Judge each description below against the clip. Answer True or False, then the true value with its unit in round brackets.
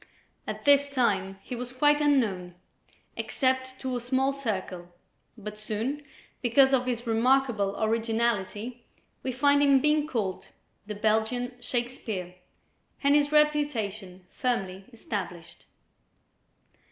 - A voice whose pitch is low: False (240 Hz)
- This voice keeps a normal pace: False (115 wpm)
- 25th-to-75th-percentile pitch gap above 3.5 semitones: True (4.3 semitones)